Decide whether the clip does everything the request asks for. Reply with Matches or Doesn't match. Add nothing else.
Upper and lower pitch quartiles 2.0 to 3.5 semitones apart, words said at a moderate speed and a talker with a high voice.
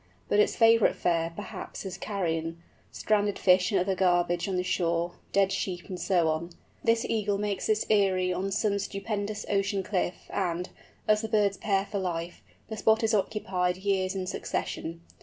Matches